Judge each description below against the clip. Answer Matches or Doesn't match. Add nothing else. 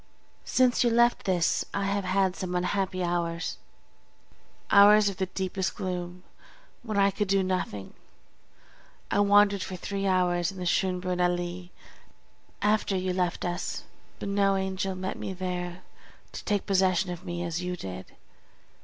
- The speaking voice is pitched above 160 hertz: Matches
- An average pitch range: Doesn't match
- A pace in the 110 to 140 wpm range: Doesn't match